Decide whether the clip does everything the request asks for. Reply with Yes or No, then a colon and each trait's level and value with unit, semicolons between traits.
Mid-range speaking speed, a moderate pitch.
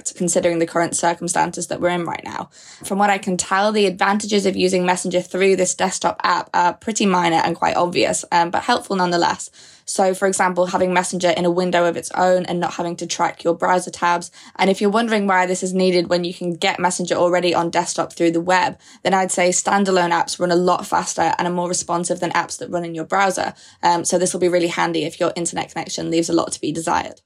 No: fast, 240 wpm; medium, 180 Hz